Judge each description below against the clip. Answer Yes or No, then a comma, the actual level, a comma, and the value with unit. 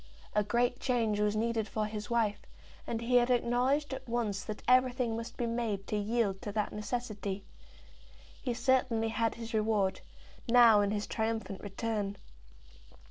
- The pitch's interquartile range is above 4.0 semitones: No, narrow, 2.4 semitones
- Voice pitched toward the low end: No, high, 225 Hz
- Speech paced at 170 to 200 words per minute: No, average, 155 wpm